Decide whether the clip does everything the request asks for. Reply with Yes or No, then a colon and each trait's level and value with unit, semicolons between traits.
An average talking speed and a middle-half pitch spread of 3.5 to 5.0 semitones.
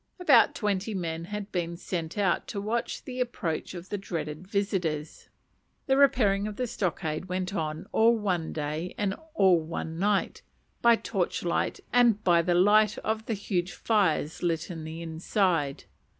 Yes: average, 155 wpm; average, 4.1 semitones